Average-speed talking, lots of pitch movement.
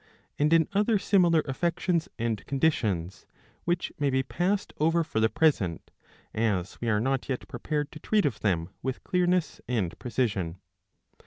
Yes: average, 160 wpm; wide, 7.3 semitones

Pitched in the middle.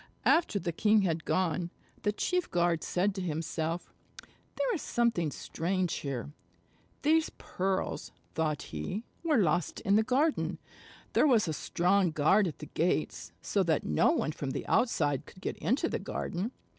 Yes: medium, 180 Hz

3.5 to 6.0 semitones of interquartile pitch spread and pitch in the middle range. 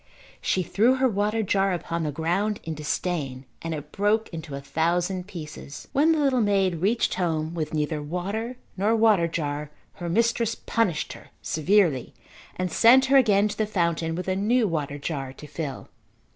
Yes: average, 5.2 semitones; medium, 180 Hz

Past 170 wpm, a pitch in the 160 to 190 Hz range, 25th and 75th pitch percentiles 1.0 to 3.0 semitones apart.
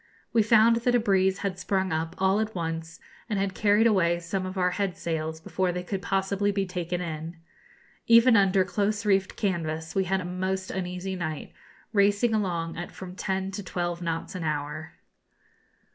Yes: average, 180 wpm; medium, 185 Hz; narrow, 2.6 semitones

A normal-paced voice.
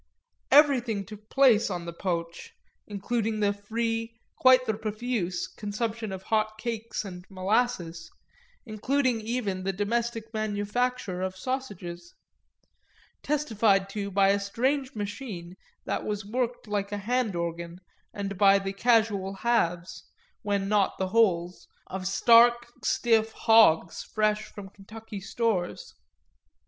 No: slow, 120 wpm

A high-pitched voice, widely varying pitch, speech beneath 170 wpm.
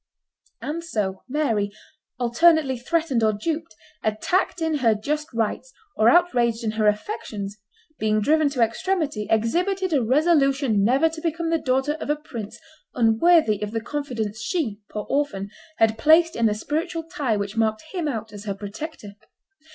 Yes: very high, 255 Hz; wide, 6.7 semitones; average, 160 wpm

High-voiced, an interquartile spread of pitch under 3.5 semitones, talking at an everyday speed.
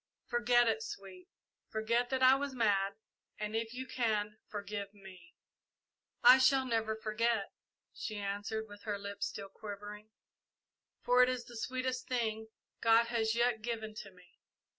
Yes: high, 220 Hz; average, 2.8 semitones; average, 150 wpm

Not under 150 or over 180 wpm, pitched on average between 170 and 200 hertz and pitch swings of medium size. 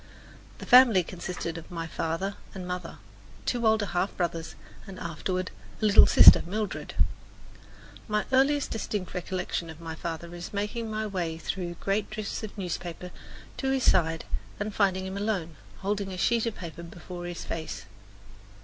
Yes: average, 160 wpm; medium, 185 Hz; average, 3.7 semitones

